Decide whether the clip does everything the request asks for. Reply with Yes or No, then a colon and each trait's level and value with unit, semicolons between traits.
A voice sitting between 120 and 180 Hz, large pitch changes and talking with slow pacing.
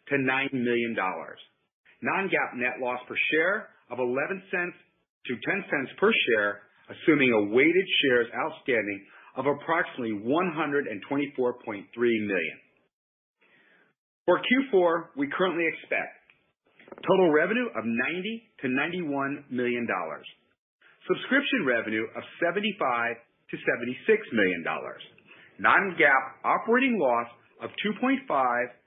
Yes: medium, 140 Hz; wide, 7.5 semitones; slow, 110 wpm